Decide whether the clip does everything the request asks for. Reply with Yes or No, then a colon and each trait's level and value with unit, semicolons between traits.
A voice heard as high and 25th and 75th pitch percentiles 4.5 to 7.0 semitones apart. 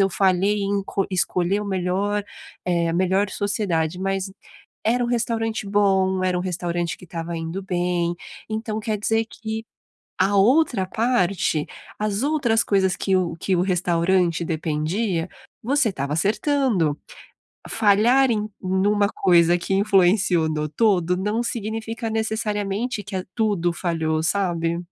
No: high, 195 Hz; average, 3.7 semitones